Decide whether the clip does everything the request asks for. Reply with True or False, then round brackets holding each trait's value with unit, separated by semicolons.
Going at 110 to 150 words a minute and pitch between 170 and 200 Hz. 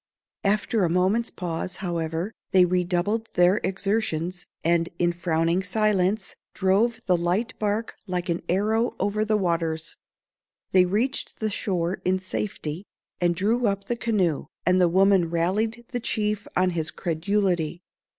True (140 wpm; 185 Hz)